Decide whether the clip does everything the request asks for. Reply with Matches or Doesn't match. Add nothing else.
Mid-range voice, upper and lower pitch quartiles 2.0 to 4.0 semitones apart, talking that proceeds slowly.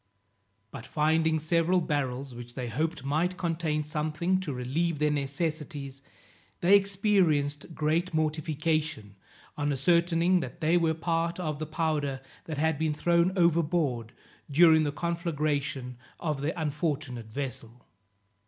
Matches